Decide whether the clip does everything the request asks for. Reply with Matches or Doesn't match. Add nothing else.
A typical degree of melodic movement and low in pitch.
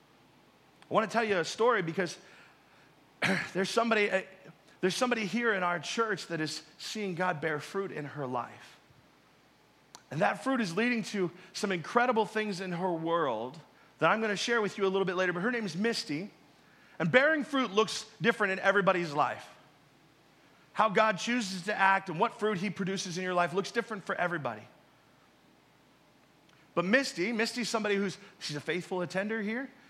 Doesn't match